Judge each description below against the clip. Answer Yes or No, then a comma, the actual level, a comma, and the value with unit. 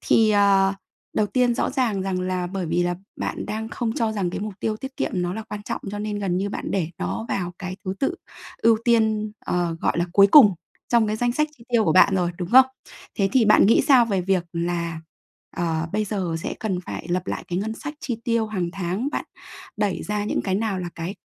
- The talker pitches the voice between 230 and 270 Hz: No, high, 200 Hz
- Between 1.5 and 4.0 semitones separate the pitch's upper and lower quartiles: Yes, average, 3.7 semitones